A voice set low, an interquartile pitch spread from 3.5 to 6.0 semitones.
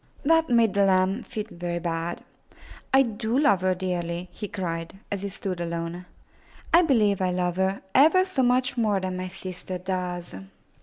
No: high, 190 Hz; average, 4.4 semitones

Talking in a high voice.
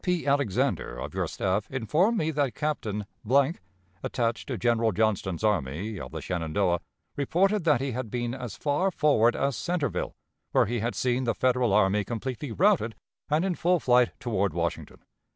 No: low, 120 Hz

